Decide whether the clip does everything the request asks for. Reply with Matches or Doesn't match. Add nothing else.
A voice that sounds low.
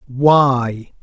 Matches